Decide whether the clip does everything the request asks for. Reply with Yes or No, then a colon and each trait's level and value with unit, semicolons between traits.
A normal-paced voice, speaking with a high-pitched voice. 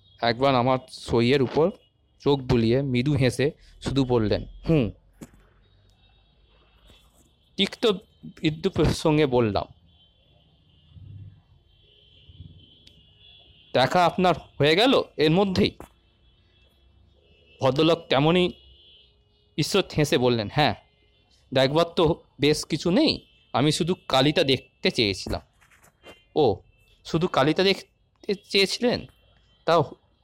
No: average, 85 wpm; low, 125 Hz